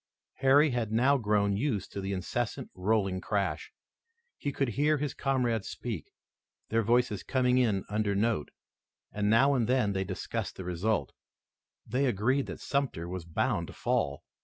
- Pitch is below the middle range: Yes, low, 110 Hz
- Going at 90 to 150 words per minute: No, average, 160 wpm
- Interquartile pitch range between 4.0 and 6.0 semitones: Yes, average, 4.7 semitones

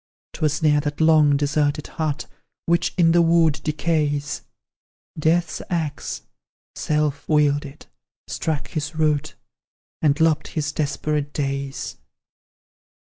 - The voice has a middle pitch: Yes, medium, 150 Hz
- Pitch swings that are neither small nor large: No, narrow, 1.6 semitones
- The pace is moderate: No, slow, 105 wpm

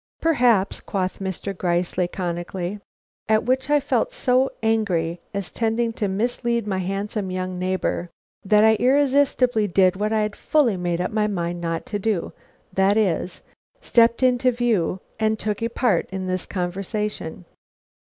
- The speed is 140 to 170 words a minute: Yes, average, 150 wpm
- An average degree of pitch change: Yes, average, 4.0 semitones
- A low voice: No, high, 205 Hz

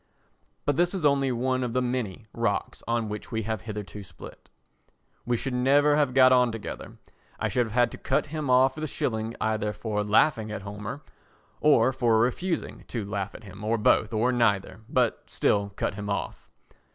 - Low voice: Yes, low, 115 Hz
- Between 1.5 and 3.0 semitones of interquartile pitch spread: No, average, 3.5 semitones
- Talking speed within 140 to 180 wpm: No, average, 190 wpm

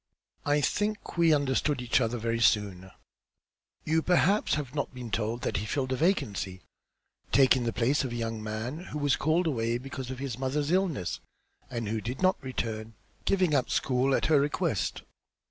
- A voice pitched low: Yes, low, 130 Hz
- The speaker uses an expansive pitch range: No, average, 4.6 semitones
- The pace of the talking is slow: No, average, 180 wpm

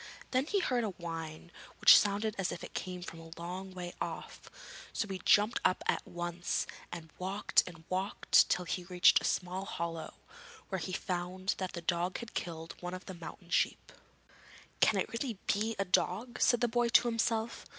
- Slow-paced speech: No, average, 190 wpm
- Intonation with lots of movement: No, average, 3.8 semitones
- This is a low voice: No, medium, 185 Hz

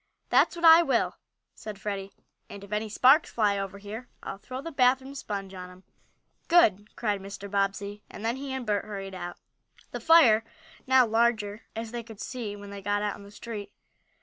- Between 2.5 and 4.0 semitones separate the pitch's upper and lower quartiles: Yes, average, 3.7 semitones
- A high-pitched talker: Yes, high, 210 Hz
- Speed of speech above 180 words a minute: Yes, average, 200 wpm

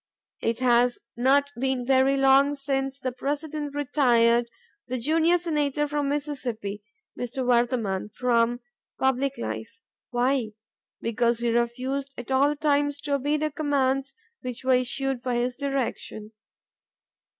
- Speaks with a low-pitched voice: No, very high, 265 Hz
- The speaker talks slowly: Yes, slow, 130 wpm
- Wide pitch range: No, average, 2.8 semitones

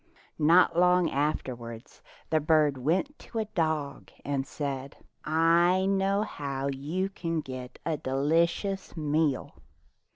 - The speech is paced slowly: Yes, slow, 125 wpm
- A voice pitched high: No, medium, 155 Hz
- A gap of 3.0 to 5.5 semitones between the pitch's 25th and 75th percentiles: Yes, average, 4.3 semitones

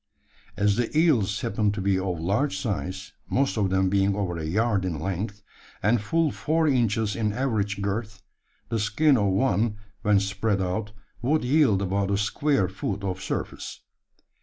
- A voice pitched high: No, low, 105 Hz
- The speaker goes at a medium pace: Yes, average, 165 wpm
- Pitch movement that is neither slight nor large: Yes, average, 3.2 semitones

